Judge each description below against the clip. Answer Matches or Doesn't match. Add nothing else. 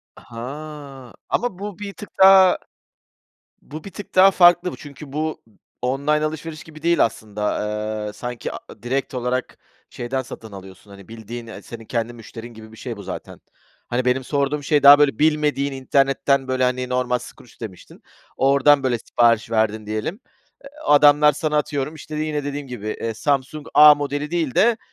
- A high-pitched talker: Doesn't match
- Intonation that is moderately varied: Matches